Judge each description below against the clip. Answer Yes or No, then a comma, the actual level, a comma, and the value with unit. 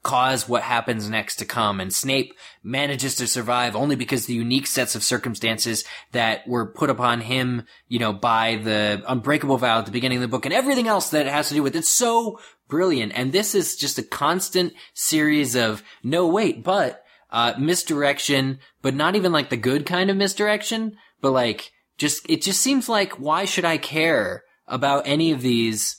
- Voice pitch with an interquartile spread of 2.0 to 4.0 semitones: No, average, 4.9 semitones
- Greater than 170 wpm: Yes, average, 195 wpm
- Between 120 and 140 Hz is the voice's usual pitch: Yes, low, 135 Hz